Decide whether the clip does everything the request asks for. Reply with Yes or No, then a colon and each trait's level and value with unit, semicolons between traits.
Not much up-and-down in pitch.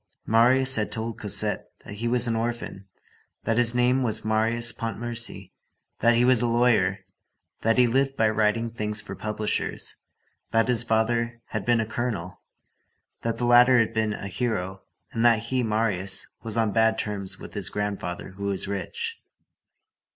Yes: narrow, 2.1 semitones